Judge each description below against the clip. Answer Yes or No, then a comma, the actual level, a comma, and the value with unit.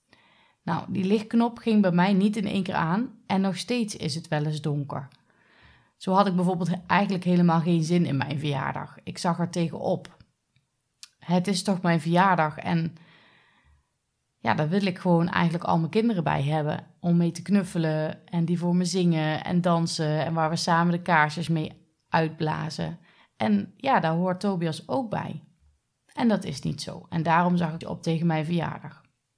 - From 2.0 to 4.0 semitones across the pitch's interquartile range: Yes, average, 2.9 semitones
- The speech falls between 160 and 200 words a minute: Yes, average, 185 wpm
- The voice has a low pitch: No, medium, 170 Hz